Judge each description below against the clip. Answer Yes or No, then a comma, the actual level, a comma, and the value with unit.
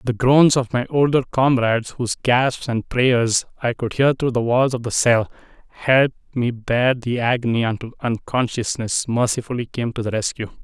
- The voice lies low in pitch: Yes, low, 120 Hz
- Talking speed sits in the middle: Yes, average, 175 wpm